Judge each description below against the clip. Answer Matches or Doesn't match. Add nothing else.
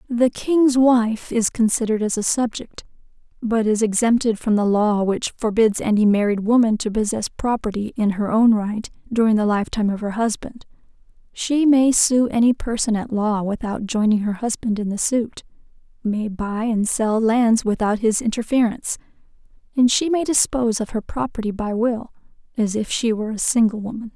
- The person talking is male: Doesn't match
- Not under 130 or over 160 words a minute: Doesn't match